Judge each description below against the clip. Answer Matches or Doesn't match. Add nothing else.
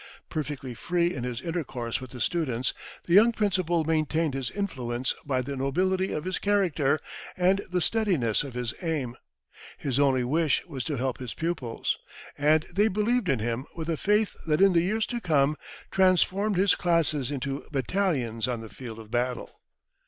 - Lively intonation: Matches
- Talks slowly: Doesn't match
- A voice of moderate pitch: Matches